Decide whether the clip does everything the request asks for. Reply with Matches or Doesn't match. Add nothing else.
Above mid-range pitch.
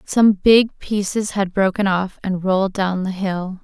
Matches